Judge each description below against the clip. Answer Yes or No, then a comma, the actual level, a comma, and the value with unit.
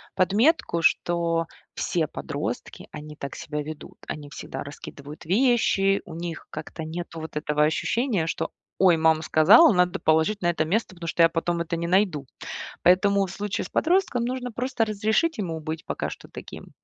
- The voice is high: No, medium, 175 Hz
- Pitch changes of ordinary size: Yes, average, 4.6 semitones